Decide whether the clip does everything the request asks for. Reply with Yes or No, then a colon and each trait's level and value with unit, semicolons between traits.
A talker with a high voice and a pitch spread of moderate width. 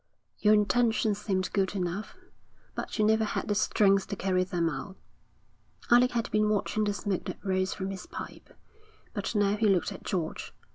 No: high, 200 Hz; narrow, 2.1 semitones